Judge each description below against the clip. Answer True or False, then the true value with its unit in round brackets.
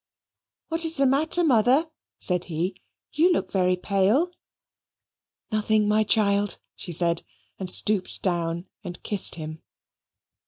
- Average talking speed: False (125 wpm)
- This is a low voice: False (205 Hz)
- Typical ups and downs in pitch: False (6.3 semitones)